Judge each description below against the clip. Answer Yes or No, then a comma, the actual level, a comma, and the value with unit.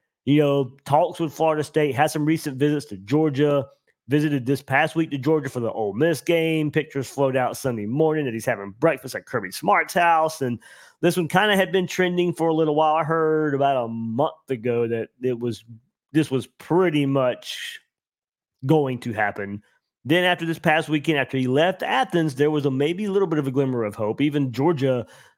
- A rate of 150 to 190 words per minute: No, fast, 205 wpm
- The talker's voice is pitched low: No, medium, 145 Hz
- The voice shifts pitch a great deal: No, average, 3.7 semitones